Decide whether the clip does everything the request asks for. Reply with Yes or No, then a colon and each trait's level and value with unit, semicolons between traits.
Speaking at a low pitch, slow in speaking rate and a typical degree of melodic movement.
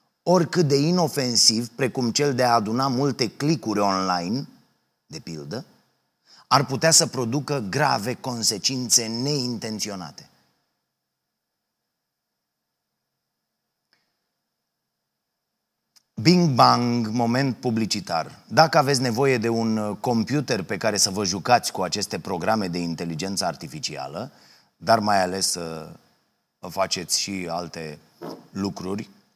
No: low, 115 Hz; slow, 100 wpm; wide, 6.1 semitones